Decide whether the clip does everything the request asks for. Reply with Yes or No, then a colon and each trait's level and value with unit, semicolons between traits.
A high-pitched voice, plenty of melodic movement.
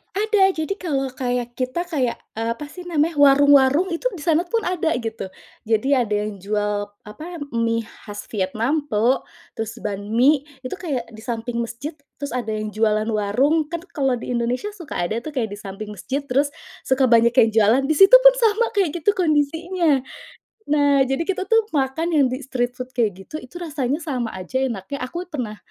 Yes: very high, 265 Hz; wide, 5.8 semitones